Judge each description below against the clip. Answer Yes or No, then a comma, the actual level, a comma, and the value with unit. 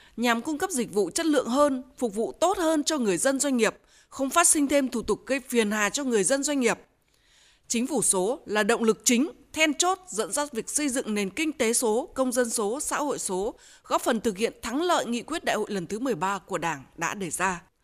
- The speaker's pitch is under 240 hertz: No, high, 245 Hz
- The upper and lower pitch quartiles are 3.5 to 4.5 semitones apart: No, average, 5.2 semitones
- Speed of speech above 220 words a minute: Yes, average, 245 wpm